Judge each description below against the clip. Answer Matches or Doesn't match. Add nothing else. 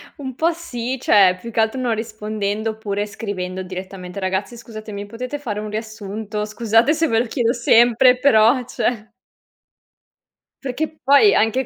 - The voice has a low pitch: Doesn't match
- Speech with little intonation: Doesn't match